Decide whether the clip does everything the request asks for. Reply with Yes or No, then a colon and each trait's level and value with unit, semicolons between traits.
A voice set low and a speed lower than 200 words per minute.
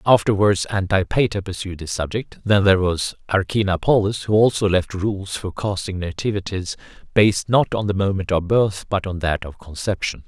Yes: very low, 95 Hz; average, 165 wpm